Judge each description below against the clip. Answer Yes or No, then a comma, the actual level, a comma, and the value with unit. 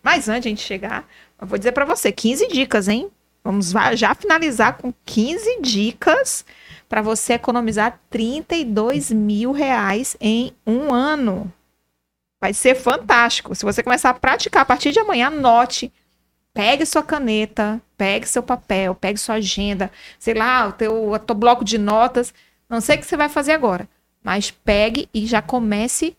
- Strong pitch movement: No, average, 3.2 semitones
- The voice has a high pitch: Yes, high, 235 Hz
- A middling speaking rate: Yes, average, 165 wpm